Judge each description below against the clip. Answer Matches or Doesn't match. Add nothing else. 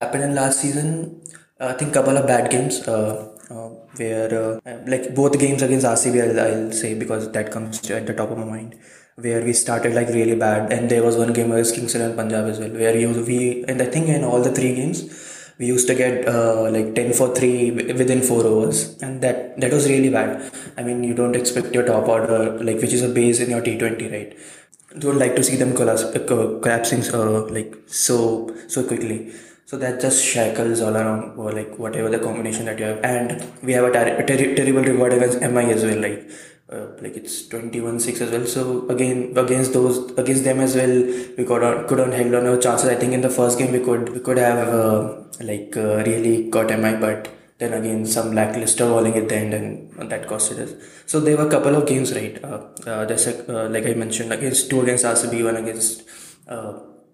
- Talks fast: Matches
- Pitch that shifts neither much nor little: Doesn't match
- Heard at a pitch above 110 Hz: Matches